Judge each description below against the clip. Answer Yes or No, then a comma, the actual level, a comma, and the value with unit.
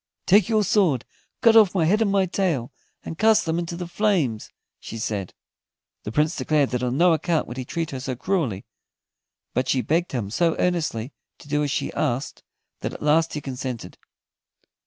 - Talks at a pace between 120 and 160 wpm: No, average, 190 wpm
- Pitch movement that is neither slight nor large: No, wide, 6.0 semitones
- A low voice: No, medium, 155 Hz